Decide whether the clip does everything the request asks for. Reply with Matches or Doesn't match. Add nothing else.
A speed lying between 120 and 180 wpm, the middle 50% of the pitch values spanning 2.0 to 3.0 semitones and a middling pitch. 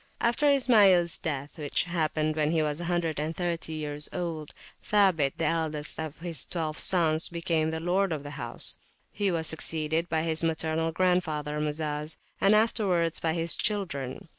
Matches